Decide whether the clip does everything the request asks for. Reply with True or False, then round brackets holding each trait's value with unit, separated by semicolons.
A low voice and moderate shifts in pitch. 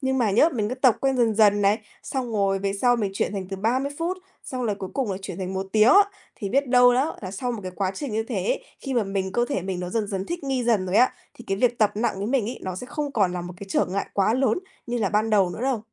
False (220 Hz; 4.5 semitones)